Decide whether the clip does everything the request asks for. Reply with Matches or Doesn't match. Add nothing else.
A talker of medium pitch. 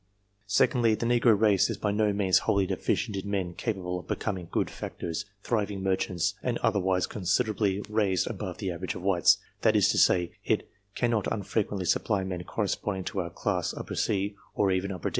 Doesn't match